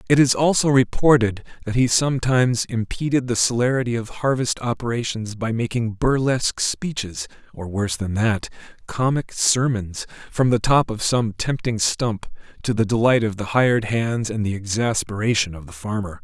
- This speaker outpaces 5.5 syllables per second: No, 5.0 syllables/s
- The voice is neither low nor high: No, low, 115 Hz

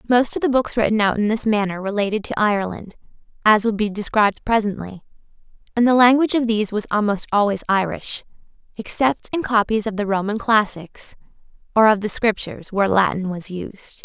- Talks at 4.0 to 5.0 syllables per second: No, 5.8 syllables/s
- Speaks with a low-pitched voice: No, high, 210 Hz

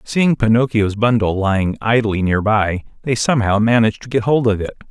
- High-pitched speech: No, low, 110 Hz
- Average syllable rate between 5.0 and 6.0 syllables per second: Yes, 5.4 syllables/s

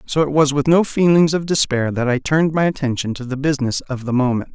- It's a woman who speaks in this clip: No, male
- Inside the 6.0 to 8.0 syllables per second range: Yes, 6.1 syllables/s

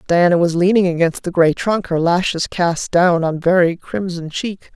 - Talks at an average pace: Yes, average, 190 wpm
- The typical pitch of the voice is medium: Yes, medium, 175 Hz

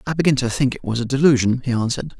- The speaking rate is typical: No, fast, 275 wpm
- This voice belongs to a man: Yes, male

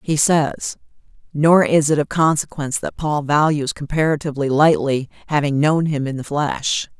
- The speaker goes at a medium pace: Yes, average, 155 wpm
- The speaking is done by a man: No, female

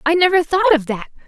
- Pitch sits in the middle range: No, very high, 320 Hz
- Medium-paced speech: No, fast, 235 wpm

